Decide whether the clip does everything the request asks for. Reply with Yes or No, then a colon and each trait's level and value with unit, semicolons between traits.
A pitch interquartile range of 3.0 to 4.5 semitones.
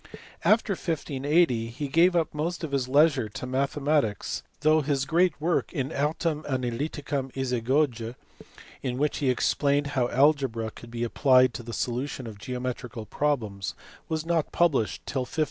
Yes: average, 3.7 semitones